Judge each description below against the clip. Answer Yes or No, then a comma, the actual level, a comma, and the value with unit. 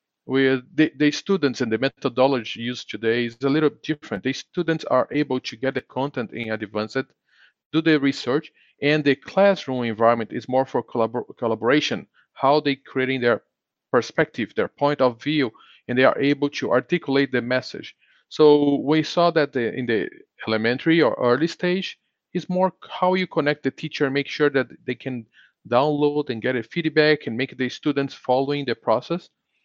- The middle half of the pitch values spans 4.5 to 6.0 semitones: No, average, 3.4 semitones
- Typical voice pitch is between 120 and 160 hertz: Yes, low, 135 Hz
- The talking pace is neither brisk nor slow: Yes, average, 175 wpm